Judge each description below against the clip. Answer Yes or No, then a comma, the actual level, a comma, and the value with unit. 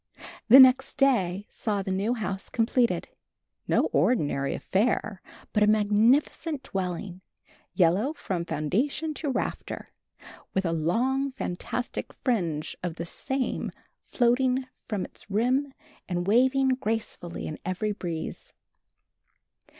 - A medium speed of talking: No, slow, 115 wpm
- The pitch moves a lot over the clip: Yes, wide, 6.0 semitones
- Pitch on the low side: No, high, 215 Hz